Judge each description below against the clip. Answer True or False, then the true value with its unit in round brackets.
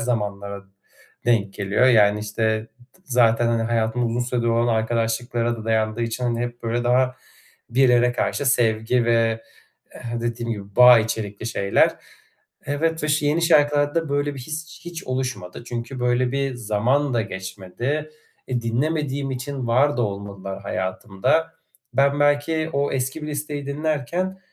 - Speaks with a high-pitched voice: False (120 Hz)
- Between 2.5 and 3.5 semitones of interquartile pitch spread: False (4.0 semitones)